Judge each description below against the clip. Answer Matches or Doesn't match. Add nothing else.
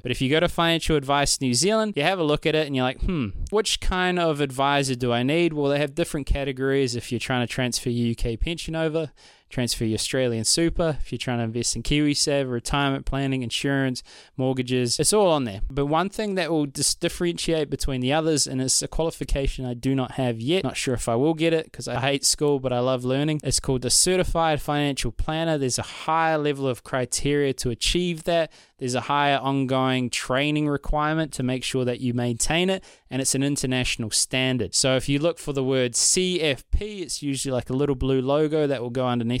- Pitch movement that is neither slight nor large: Matches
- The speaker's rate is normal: Doesn't match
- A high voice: Doesn't match